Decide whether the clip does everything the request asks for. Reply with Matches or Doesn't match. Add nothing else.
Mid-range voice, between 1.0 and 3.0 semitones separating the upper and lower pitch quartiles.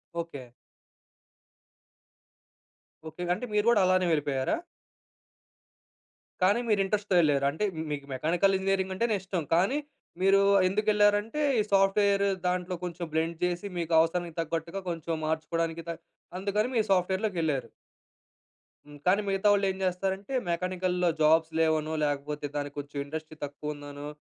Doesn't match